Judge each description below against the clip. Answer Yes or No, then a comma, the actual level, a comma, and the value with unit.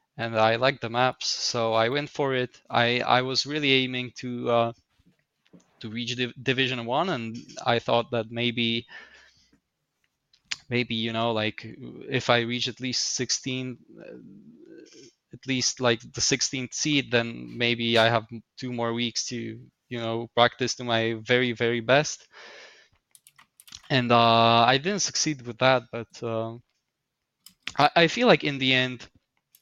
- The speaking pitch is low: Yes, low, 120 Hz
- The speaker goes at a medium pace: Yes, average, 150 wpm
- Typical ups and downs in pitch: No, narrow, 1.8 semitones